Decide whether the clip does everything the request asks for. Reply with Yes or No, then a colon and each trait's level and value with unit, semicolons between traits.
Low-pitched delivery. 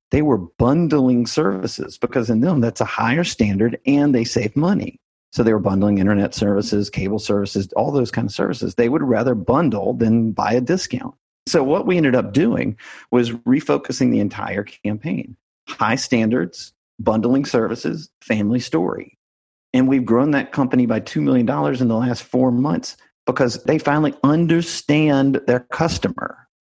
Yes: low, 120 Hz